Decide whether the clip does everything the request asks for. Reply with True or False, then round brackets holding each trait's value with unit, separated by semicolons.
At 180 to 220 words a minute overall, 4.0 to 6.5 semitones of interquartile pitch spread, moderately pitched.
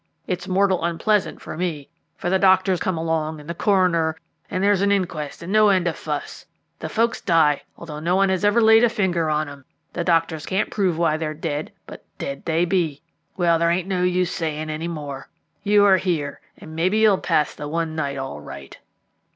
False (205 wpm; 3.4 semitones; 170 Hz)